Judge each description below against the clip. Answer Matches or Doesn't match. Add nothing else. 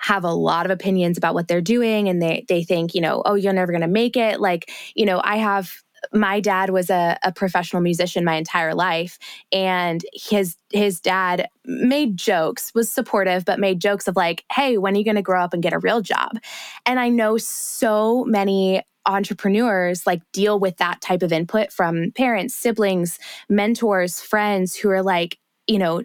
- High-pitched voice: Matches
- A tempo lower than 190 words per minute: Doesn't match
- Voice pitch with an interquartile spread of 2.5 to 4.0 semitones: Matches